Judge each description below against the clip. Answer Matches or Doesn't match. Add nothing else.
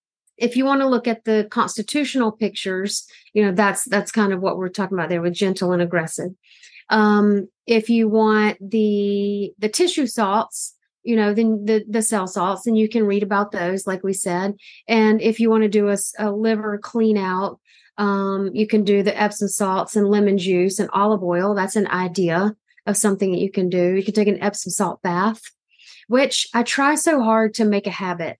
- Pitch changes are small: Matches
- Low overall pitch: Doesn't match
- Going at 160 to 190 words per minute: Doesn't match